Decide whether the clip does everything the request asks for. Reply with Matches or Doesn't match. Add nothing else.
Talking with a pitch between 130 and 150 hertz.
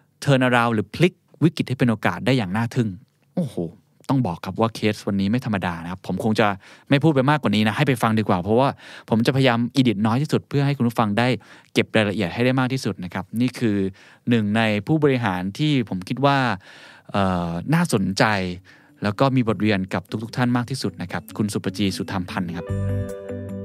Doesn't match